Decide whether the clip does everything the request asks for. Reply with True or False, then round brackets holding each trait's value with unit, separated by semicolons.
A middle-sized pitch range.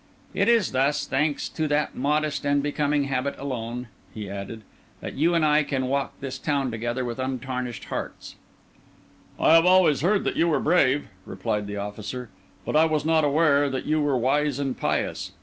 True (3.1 semitones)